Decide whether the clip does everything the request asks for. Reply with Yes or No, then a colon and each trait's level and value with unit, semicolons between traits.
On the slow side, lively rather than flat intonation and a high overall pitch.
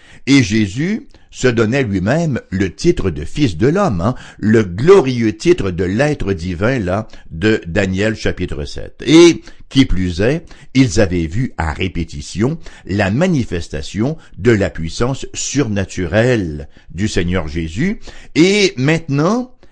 No: slow, 130 wpm; wide, 7.3 semitones; low, 110 Hz